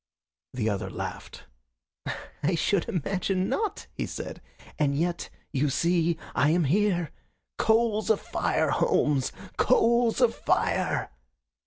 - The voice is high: No, medium, 180 Hz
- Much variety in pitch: Yes, wide, 6.7 semitones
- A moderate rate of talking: No, slow, 120 wpm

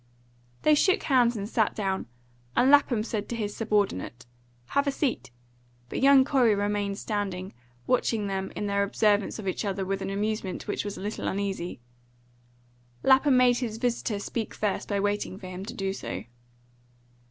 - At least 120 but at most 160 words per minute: No, average, 170 wpm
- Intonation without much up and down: No, average, 3.6 semitones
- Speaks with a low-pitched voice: No, high, 210 Hz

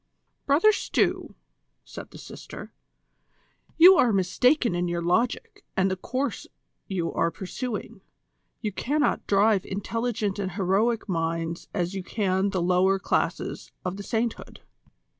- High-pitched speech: Yes, high, 195 Hz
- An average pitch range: Yes, average, 4.4 semitones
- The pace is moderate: No, slow, 130 wpm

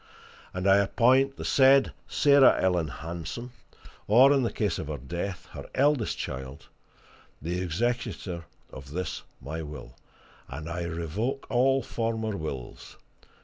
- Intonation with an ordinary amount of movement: No, wide, 7.4 semitones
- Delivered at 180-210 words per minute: No, slow, 135 wpm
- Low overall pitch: Yes, very low, 95 Hz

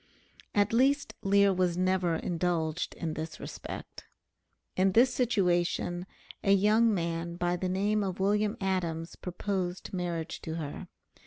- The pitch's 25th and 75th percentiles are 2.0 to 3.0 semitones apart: Yes, average, 2.7 semitones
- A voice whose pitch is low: No, medium, 185 Hz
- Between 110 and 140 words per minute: Yes, slow, 135 wpm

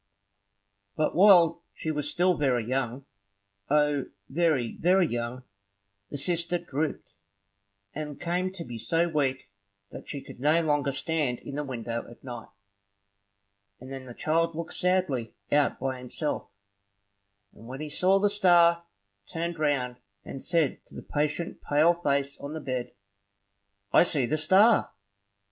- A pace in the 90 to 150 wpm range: Yes, average, 145 wpm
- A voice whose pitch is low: No, medium, 150 Hz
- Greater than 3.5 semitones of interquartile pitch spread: Yes, average, 4.3 semitones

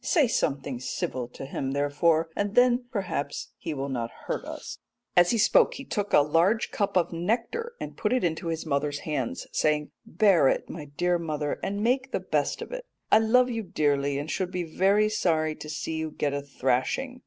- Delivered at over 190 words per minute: Yes, average, 200 wpm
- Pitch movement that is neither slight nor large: No, wide, 6.7 semitones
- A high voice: No, medium, 165 Hz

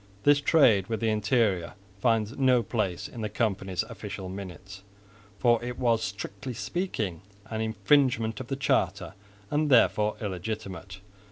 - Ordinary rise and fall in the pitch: Yes, average, 3.9 semitones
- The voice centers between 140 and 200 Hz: No, low, 110 Hz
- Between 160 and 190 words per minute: No, average, 140 wpm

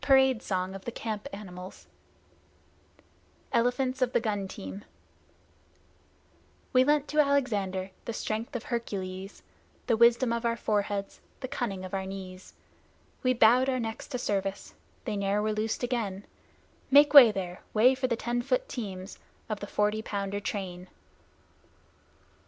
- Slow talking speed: No, average, 145 wpm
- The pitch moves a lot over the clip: No, average, 4.1 semitones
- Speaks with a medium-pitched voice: No, high, 220 Hz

